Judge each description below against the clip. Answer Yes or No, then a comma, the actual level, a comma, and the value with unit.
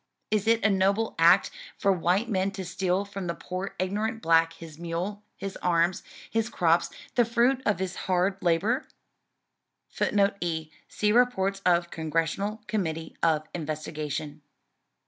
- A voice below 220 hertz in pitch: Yes, medium, 185 Hz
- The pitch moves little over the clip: No, average, 3.9 semitones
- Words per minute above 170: No, average, 145 wpm